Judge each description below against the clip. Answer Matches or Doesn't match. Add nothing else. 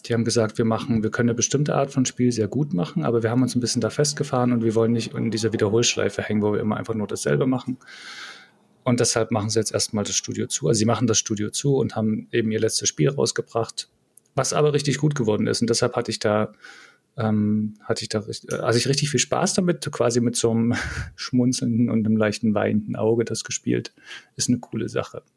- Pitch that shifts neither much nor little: Doesn't match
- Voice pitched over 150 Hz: Doesn't match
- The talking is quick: Matches